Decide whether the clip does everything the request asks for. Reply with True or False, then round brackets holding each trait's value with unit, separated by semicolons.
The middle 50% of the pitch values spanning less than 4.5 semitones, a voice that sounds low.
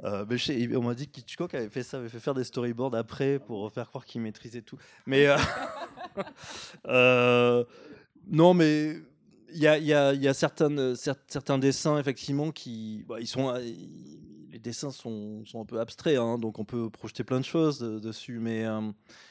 True (3.5 semitones; 125 Hz)